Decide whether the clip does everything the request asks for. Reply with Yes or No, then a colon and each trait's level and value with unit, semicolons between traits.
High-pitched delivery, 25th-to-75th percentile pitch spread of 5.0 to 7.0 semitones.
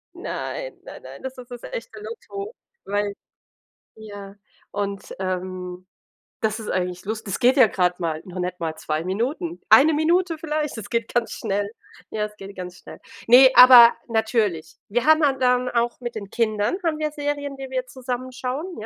Yes: high, 235 Hz; wide, 5.5 semitones